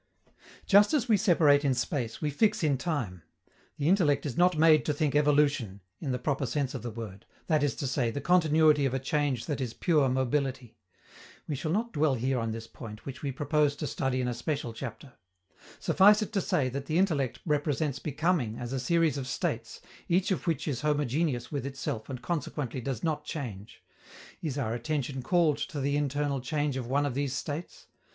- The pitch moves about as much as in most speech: Yes, average, 3.4 semitones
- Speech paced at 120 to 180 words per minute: No, average, 200 wpm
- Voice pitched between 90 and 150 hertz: Yes, medium, 140 Hz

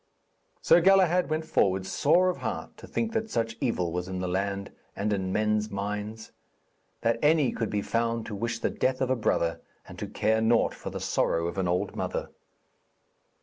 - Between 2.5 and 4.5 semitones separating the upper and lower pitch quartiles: No, average, 5.0 semitones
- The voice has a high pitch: No, low, 110 Hz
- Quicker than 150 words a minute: Yes, average, 190 wpm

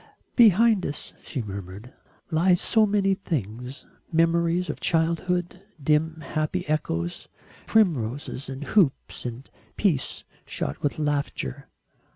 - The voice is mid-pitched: Yes, medium, 155 Hz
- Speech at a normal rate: No, slow, 110 wpm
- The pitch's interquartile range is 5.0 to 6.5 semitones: Yes, wide, 5.4 semitones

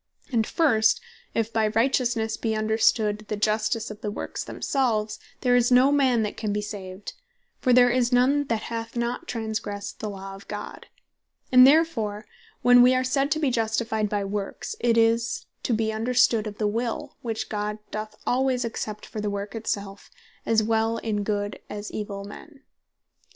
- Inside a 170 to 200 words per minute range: Yes, average, 180 wpm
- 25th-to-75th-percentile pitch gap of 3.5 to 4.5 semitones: No, average, 2.7 semitones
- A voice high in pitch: Yes, high, 220 Hz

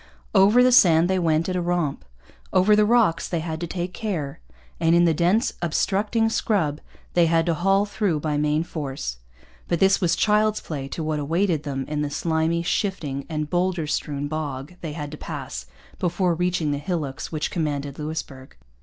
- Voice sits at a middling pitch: Yes, medium, 165 Hz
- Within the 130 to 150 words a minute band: No, average, 185 wpm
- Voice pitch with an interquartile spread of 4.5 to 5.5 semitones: No, average, 3.7 semitones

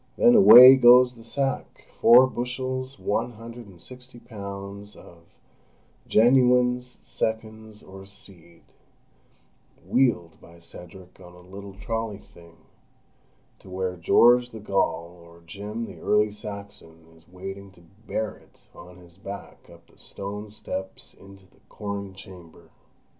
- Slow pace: Yes, slow, 125 wpm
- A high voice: No, low, 100 Hz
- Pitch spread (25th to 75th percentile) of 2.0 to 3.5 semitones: No, average, 4.5 semitones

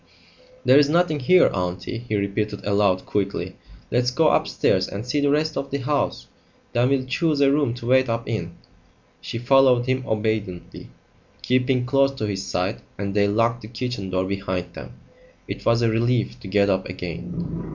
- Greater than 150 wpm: Yes, average, 175 wpm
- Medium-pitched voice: No, low, 120 Hz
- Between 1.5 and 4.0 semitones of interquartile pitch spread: No, average, 5.1 semitones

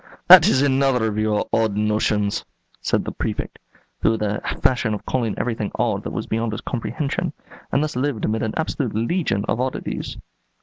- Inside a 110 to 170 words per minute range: No, average, 180 wpm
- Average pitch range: Yes, average, 4.2 semitones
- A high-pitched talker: No, low, 115 Hz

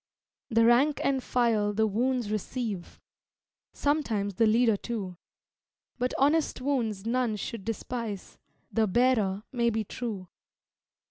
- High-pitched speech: Yes, high, 230 Hz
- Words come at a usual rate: No, slow, 120 wpm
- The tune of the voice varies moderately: Yes, average, 3.2 semitones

